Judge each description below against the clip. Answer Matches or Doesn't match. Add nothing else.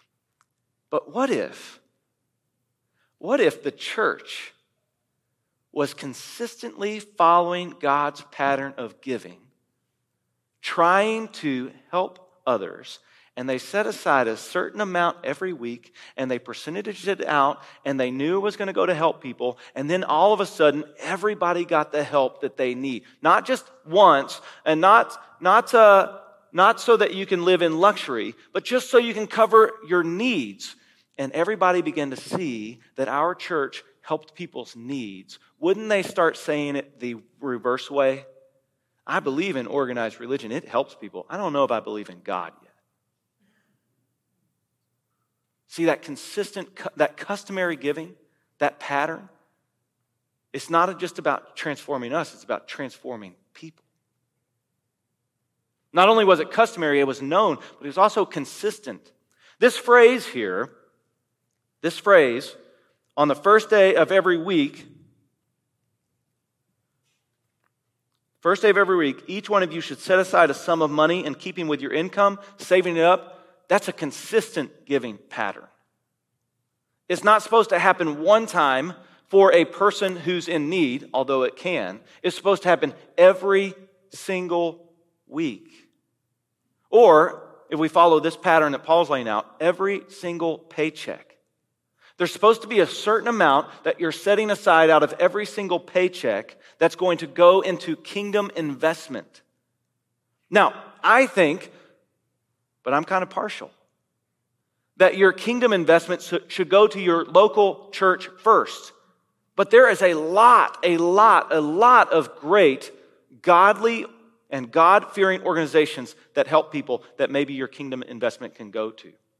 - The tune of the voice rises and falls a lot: Matches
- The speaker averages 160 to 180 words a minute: Doesn't match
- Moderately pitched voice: Matches